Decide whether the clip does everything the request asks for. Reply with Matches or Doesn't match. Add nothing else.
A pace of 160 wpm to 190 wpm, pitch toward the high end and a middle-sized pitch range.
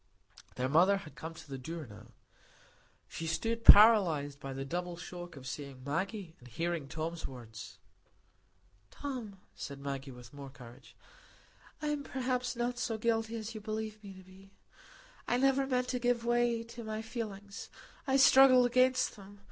Doesn't match